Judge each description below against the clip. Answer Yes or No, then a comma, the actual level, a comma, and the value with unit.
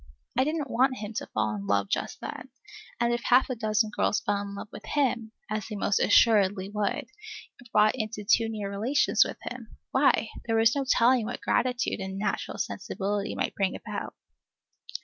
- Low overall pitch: No, high, 220 Hz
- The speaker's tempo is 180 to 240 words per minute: Yes, average, 190 wpm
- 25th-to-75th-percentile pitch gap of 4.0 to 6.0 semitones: No, average, 3.3 semitones